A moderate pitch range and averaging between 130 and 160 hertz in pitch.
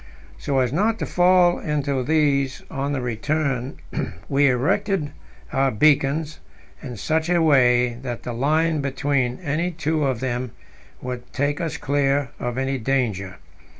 Yes: average, 3.5 semitones; medium, 140 Hz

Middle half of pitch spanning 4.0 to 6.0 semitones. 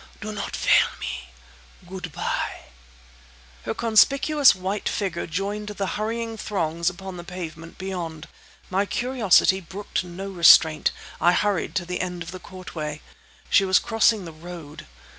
No: average, 3.4 semitones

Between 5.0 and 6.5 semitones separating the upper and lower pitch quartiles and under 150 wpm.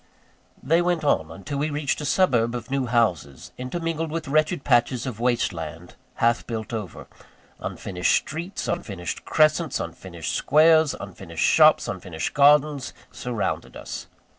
Yes: wide, 5.5 semitones; average, 140 wpm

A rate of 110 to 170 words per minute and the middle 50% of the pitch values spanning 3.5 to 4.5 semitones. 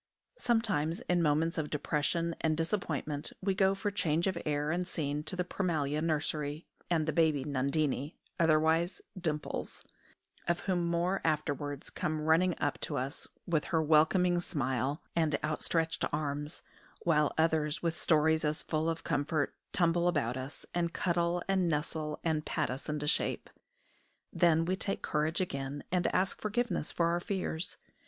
No: average, 155 wpm; narrow, 2.6 semitones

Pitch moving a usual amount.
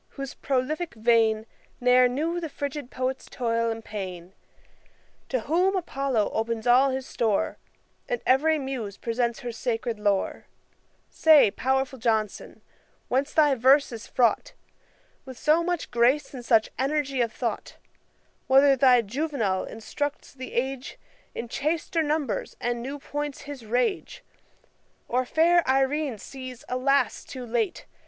Yes: average, 3.7 semitones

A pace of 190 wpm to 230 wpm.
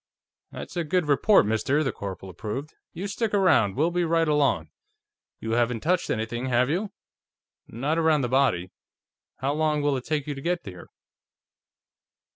No: average, 165 wpm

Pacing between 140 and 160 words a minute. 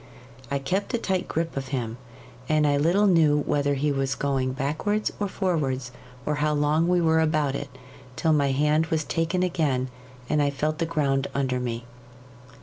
No: average, 180 wpm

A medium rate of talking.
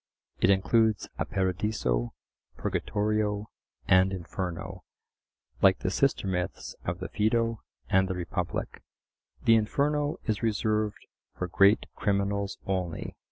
No: slow, 115 wpm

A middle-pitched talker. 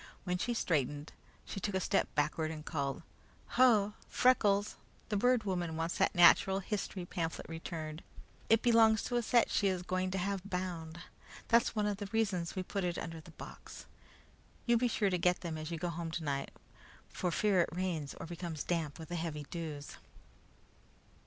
Yes: medium, 180 Hz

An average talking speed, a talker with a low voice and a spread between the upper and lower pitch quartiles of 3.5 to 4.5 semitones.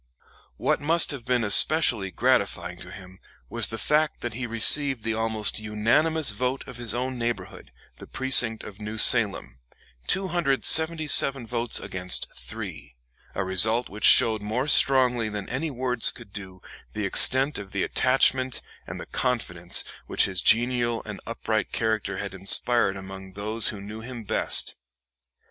Yes: average, 150 wpm; low, 115 Hz; average, 4.2 semitones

